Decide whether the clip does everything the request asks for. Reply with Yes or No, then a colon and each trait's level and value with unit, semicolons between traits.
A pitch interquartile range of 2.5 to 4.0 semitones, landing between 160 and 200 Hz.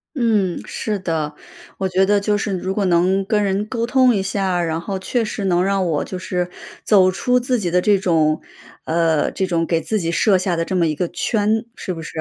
Yes: average, 3.2 semitones; high, 190 Hz